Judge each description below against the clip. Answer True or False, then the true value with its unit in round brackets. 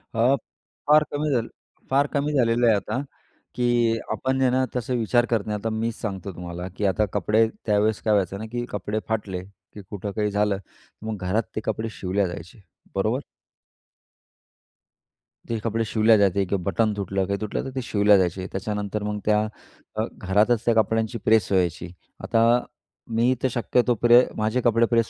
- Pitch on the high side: False (110 Hz)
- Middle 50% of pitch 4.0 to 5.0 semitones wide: False (2.7 semitones)